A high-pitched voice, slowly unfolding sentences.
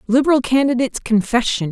Yes: high, 245 Hz; slow, 105 wpm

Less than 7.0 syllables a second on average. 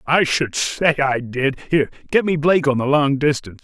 Yes: 5.3 syllables/s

